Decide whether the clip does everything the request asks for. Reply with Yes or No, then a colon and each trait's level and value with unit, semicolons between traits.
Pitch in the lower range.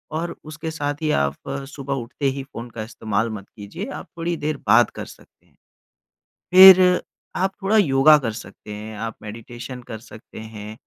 Yes: low, 125 Hz